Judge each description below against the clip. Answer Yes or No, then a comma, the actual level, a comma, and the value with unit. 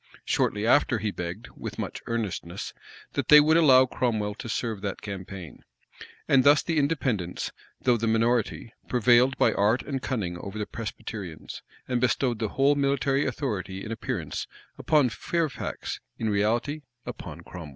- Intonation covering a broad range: No, average, 4.7 semitones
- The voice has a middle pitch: No, low, 115 Hz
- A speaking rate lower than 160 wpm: Yes, average, 150 wpm